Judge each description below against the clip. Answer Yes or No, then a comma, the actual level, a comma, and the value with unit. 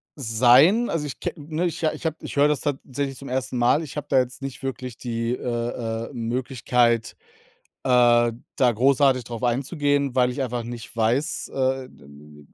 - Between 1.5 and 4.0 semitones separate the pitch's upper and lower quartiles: Yes, average, 2.9 semitones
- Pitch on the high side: No, low, 125 Hz